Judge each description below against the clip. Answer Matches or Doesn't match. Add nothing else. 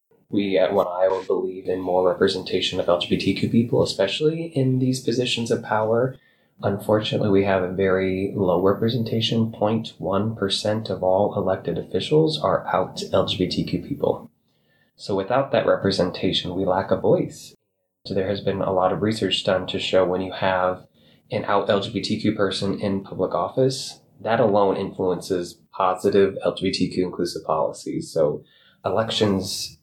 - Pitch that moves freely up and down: Doesn't match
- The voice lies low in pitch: Matches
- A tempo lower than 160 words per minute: Matches